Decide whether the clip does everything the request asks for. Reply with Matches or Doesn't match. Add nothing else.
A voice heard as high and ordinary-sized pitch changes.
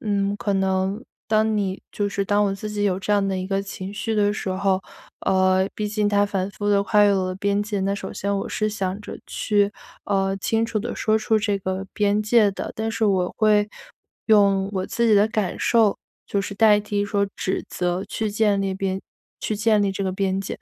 Doesn't match